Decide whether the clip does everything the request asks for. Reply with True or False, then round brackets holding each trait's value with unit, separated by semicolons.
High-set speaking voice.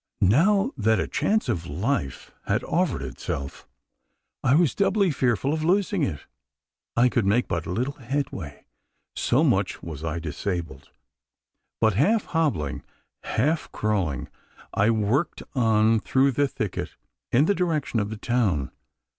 False (115 Hz)